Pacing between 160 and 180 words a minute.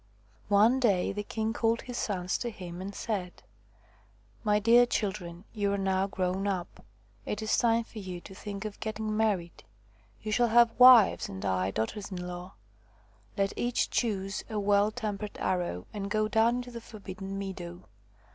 Yes: average, 175 wpm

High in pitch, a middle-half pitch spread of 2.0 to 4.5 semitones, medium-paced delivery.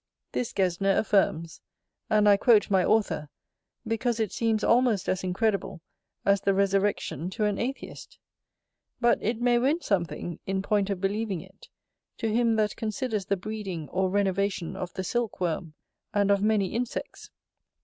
Yes: high, 200 Hz; average, 2.7 semitones; average, 155 wpm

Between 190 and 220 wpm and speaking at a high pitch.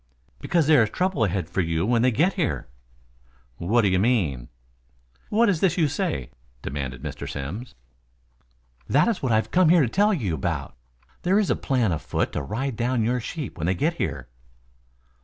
No: average, 195 wpm; low, 120 Hz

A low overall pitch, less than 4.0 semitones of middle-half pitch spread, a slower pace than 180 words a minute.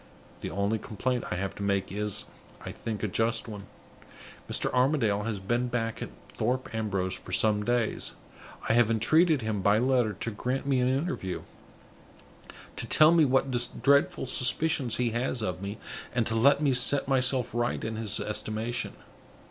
Yes: low, 115 Hz; average, 3.5 semitones; average, 170 wpm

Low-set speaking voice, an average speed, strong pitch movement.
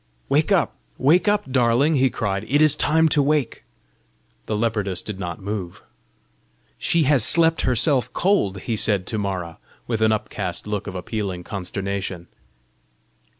Yes: low, 110 Hz; average, 150 wpm; wide, 6.5 semitones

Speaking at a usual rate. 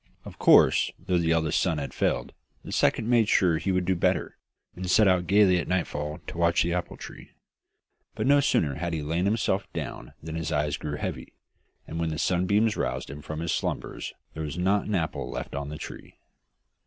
No: fast, 210 wpm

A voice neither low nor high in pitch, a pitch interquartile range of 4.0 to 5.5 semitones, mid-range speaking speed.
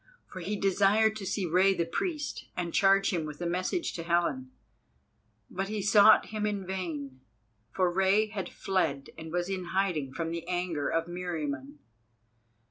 No: medium, 180 Hz; average, 3.1 semitones; average, 165 wpm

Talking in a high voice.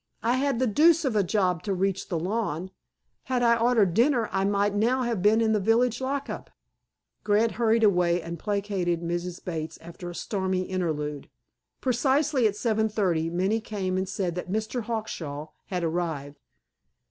Yes: high, 200 Hz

